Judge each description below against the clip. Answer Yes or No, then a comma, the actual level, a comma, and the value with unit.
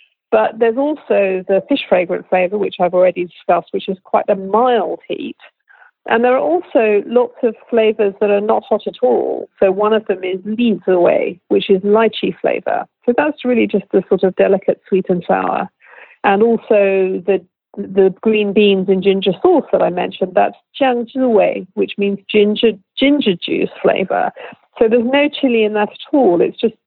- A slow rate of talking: No, average, 185 wpm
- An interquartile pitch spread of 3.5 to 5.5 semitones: Yes, average, 3.8 semitones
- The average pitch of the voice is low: No, high, 210 Hz